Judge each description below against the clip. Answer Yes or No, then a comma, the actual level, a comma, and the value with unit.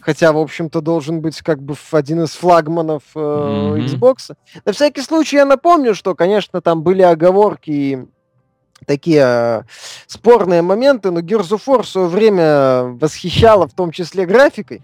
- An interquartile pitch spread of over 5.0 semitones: Yes, wide, 5.4 semitones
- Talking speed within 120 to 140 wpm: No, fast, 160 wpm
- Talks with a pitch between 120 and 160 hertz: No, medium, 170 Hz